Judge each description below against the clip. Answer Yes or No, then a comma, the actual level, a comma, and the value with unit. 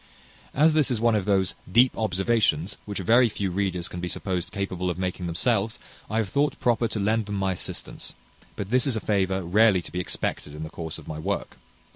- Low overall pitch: Yes, low, 100 Hz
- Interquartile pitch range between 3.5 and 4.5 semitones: Yes, average, 3.8 semitones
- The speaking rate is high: Yes, fast, 215 wpm